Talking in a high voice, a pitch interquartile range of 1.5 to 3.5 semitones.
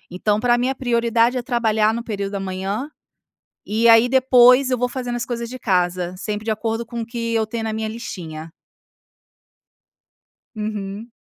Yes: high, 230 Hz; narrow, 2.5 semitones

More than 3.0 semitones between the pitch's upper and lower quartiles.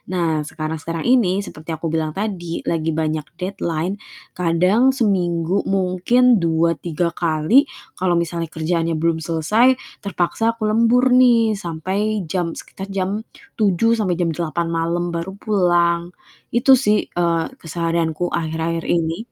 Yes: average, 3.5 semitones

